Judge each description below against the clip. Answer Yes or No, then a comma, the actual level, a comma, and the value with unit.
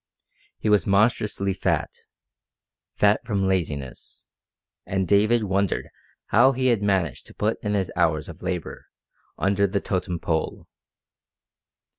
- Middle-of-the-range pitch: No, low, 100 Hz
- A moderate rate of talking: No, slow, 125 wpm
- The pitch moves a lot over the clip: No, average, 2.7 semitones